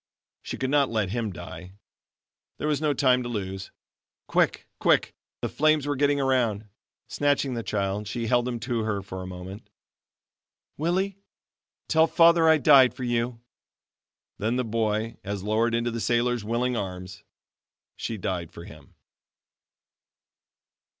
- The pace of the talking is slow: No, average, 145 wpm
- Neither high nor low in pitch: No, low, 115 Hz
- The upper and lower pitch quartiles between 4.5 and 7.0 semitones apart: Yes, average, 4.8 semitones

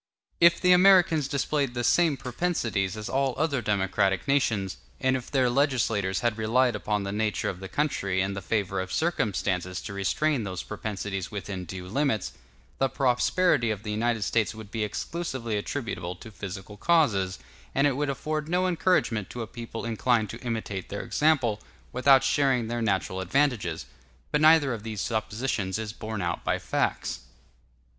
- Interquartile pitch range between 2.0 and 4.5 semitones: No, wide, 5.6 semitones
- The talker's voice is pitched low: Yes, low, 115 Hz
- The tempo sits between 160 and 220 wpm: Yes, average, 165 wpm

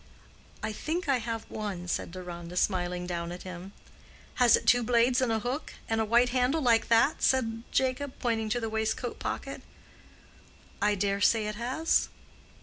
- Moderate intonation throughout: Yes, average, 4.0 semitones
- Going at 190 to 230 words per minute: No, average, 165 wpm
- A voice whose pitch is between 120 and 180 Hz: No, high, 225 Hz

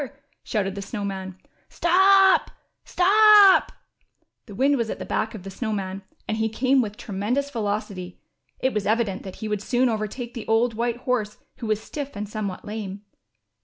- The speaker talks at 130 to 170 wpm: No, average, 180 wpm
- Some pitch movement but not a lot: Yes, average, 4.0 semitones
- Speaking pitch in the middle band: No, high, 220 Hz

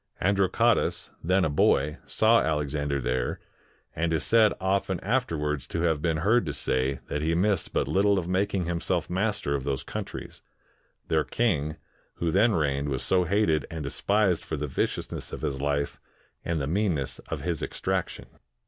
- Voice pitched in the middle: No, very low, 80 Hz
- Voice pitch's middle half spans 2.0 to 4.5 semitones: No, average, 4.9 semitones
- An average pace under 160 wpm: No, average, 170 wpm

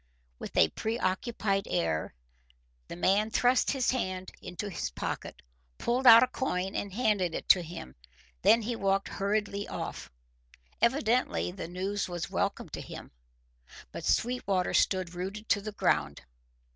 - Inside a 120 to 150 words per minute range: Yes, average, 145 wpm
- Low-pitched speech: No, high, 200 Hz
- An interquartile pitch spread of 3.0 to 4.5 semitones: Yes, average, 3.7 semitones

